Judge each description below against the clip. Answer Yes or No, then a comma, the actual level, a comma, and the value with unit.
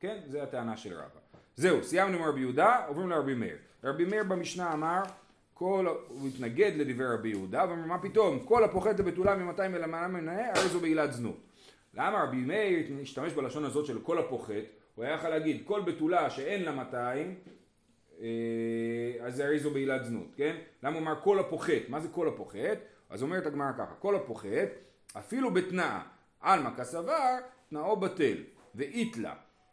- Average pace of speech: No, fast, 170 wpm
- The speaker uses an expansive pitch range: Yes, wide, 6.3 semitones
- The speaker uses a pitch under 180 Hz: Yes, medium, 160 Hz